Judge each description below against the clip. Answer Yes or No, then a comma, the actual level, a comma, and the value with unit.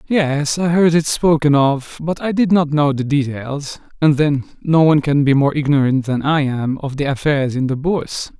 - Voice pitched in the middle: Yes, medium, 145 Hz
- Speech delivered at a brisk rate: Yes, fast, 215 wpm